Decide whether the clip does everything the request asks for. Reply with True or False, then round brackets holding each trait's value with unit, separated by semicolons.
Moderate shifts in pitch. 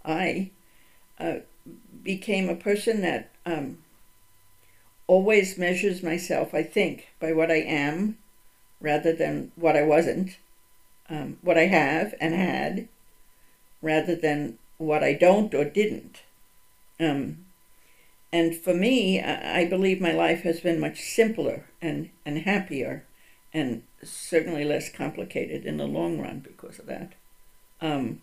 True (3.8 semitones)